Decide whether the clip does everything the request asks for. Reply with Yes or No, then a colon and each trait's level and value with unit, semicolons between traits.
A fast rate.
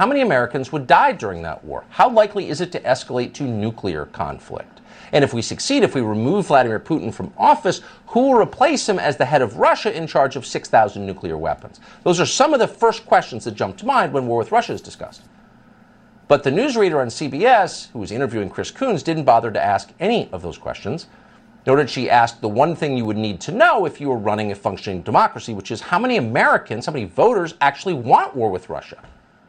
Yes: fast, 225 wpm